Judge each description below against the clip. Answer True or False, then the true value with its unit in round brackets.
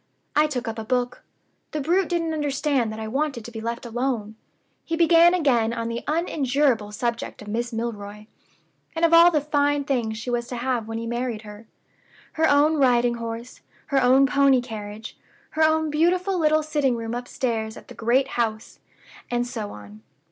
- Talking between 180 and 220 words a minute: True (185 wpm)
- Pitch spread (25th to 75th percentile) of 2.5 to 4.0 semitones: False (4.7 semitones)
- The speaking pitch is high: True (245 Hz)